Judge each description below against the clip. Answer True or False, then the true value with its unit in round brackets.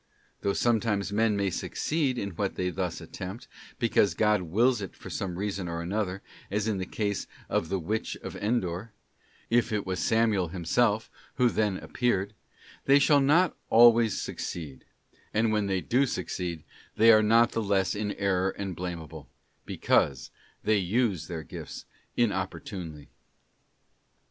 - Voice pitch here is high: False (100 Hz)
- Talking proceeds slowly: False (145 wpm)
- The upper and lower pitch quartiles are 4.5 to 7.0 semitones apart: False (3.8 semitones)